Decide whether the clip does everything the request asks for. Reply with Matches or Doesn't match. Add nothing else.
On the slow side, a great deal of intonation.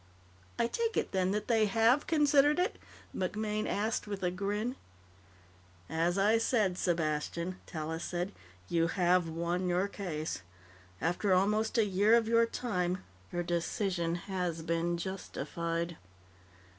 Doesn't match